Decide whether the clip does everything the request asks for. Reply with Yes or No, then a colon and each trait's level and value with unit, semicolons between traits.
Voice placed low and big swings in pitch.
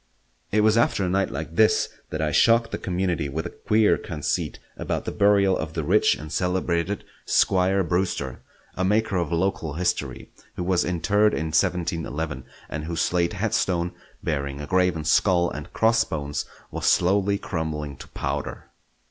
No: very low, 90 Hz; average, 3.6 semitones